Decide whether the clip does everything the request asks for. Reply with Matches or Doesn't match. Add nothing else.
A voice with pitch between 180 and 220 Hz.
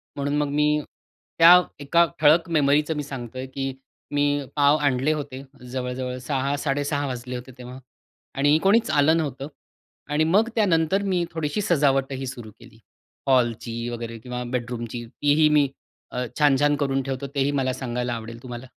Doesn't match